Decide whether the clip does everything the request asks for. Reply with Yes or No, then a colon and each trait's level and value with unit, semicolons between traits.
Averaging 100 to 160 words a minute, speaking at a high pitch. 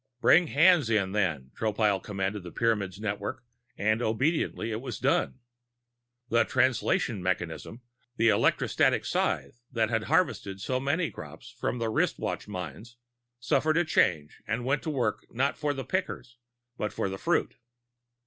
No: average, 150 wpm; low, 115 Hz